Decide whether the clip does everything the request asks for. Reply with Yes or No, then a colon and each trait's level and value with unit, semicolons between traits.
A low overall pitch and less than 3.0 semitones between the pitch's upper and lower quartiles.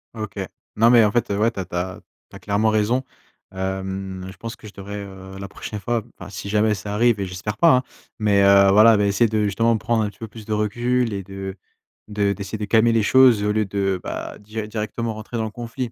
Yes: low, 105 Hz; narrow, 2.5 semitones